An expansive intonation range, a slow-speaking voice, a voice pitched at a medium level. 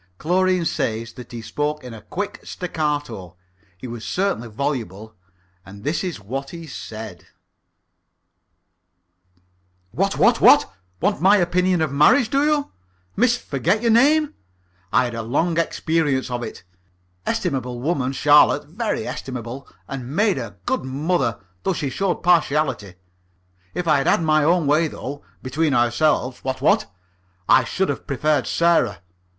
No: wide, 6.1 semitones; average, 145 wpm; medium, 145 Hz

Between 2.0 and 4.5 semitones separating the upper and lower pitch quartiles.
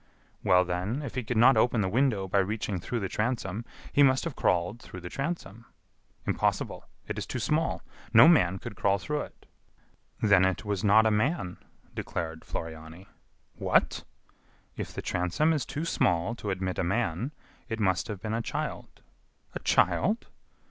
No: average, 5.2 semitones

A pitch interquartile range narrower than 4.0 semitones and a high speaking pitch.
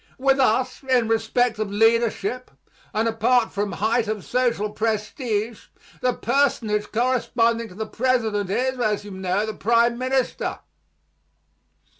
Yes: average, 2.9 semitones; high, 225 Hz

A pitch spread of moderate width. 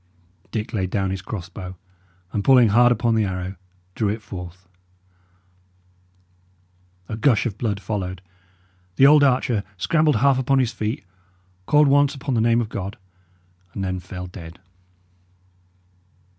Yes: average, 4.9 semitones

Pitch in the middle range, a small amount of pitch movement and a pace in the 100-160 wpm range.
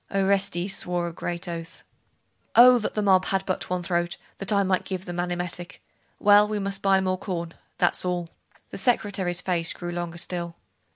No: medium, 180 Hz; narrow, 2.1 semitones; average, 185 wpm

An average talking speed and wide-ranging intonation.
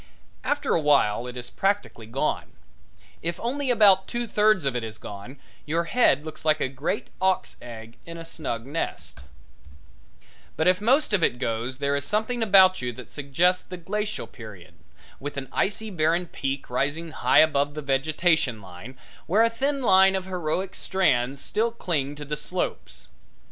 Yes: average, 170 wpm; wide, 6.3 semitones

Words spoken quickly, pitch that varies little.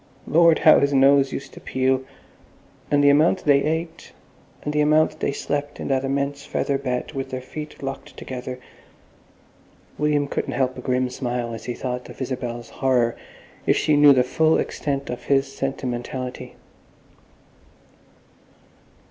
No: average, 150 wpm; narrow, 2.2 semitones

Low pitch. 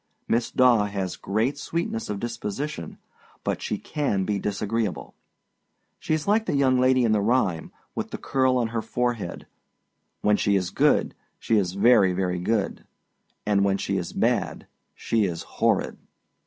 Yes: low, 110 Hz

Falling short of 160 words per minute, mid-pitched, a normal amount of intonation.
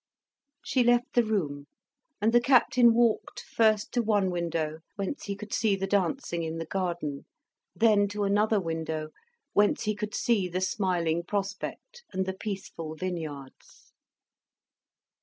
No: average, 140 wpm; high, 195 Hz; average, 4.5 semitones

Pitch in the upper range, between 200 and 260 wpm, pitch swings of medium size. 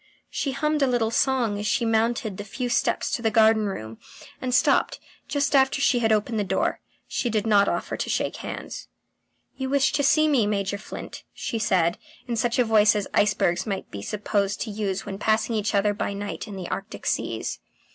Yes: high, 220 Hz; fast, 205 wpm; average, 3.3 semitones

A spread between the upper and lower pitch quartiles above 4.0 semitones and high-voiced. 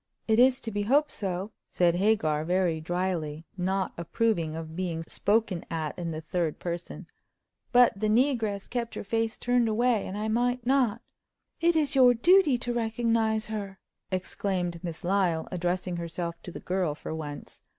Yes: average, 5.1 semitones; high, 195 Hz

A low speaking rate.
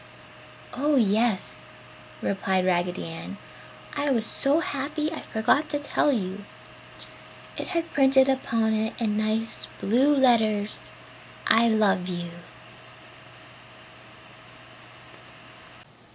Yes: slow, 95 wpm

